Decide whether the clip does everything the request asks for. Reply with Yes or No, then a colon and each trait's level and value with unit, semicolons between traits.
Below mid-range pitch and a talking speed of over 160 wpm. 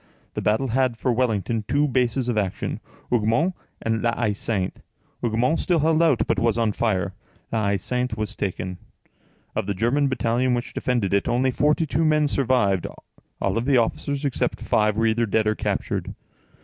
Yes: low, 120 Hz; average, 175 wpm